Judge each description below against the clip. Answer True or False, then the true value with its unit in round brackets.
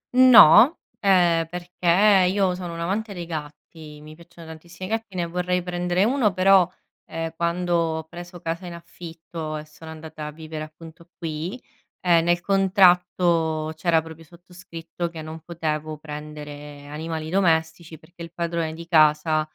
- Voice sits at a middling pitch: True (170 Hz)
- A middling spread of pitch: False (2.1 semitones)